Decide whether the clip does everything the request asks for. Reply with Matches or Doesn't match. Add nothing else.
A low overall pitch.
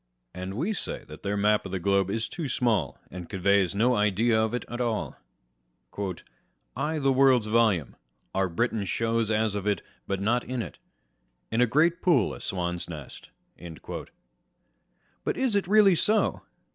Matches